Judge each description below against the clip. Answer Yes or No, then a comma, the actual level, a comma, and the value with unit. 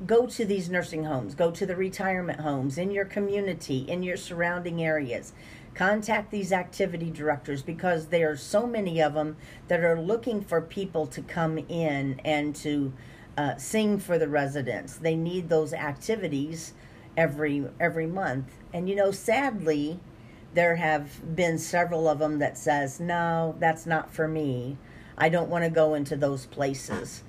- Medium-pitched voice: Yes, medium, 165 Hz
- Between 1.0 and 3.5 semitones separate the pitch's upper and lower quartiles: Yes, average, 3.2 semitones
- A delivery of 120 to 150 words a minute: No, average, 165 wpm